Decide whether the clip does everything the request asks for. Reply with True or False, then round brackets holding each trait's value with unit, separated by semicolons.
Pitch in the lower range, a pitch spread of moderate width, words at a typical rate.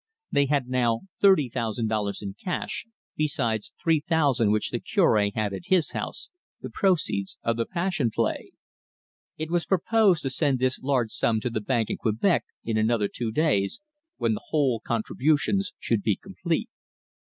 False (130 Hz; 6.6 semitones; 165 wpm)